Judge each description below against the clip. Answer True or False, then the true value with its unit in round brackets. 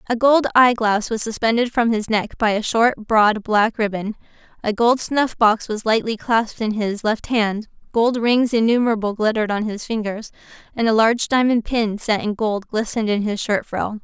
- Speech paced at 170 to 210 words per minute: True (195 wpm)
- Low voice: False (220 Hz)